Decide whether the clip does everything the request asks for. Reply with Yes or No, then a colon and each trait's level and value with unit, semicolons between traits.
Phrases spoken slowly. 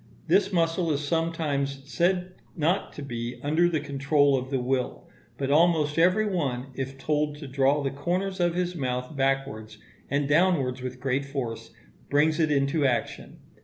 No: average, 165 wpm